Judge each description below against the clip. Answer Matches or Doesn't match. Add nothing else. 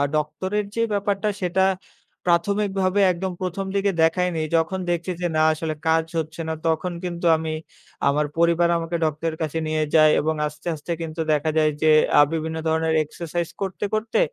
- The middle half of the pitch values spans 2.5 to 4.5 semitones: Matches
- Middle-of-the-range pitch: Matches